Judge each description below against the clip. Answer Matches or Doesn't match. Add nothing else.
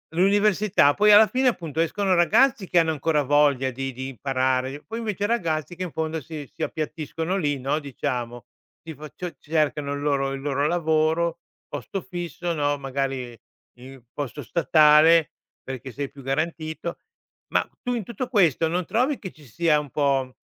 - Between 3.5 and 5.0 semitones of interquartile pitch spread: Matches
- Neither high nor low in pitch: Matches